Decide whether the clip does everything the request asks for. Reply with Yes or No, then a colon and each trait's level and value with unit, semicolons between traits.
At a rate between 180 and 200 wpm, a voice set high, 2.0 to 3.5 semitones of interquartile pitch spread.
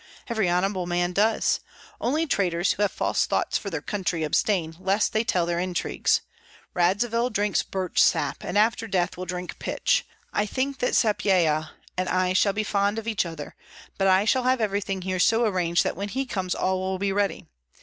Yes: average, 190 wpm; high, 195 Hz; average, 3.1 semitones